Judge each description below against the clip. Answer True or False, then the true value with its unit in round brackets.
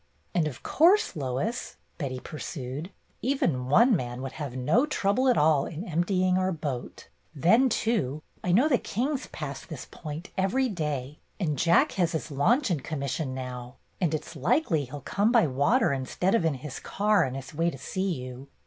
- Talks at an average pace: True (185 wpm)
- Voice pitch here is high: False (160 Hz)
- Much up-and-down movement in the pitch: True (6.7 semitones)